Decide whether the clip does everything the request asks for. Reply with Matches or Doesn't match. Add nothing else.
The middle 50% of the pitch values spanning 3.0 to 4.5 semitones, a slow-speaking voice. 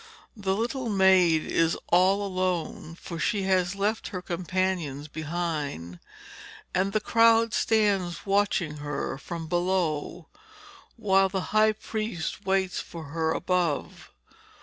Matches